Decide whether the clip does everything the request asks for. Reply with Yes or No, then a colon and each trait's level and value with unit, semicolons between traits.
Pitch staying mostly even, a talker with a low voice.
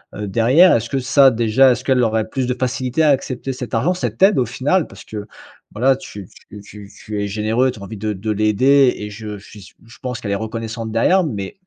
No: average, 3.8 semitones; low, 115 Hz